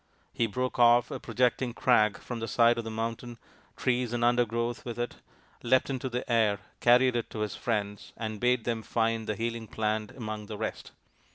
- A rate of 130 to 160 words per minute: No, average, 190 wpm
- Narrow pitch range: Yes, narrow, 1.7 semitones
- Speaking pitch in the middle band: No, low, 115 Hz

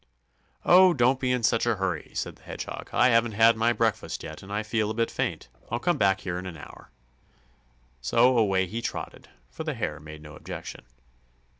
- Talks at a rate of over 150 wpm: Yes, average, 200 wpm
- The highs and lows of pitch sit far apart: No, average, 4.0 semitones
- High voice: No, low, 110 Hz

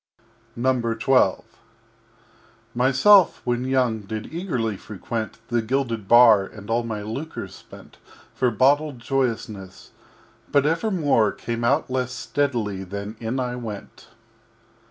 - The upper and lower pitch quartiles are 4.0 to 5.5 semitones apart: No, average, 3.4 semitones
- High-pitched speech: No, low, 120 Hz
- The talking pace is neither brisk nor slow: No, slow, 115 wpm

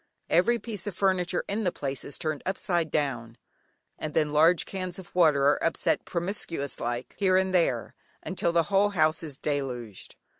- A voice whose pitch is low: No, medium, 165 Hz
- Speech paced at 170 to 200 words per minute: Yes, average, 175 wpm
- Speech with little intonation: No, average, 4.7 semitones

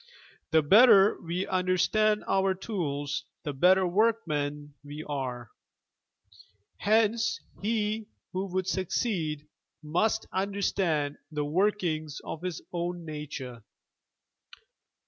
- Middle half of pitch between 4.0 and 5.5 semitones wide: Yes, average, 5.2 semitones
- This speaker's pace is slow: Yes, slow, 95 wpm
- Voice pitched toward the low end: No, medium, 180 Hz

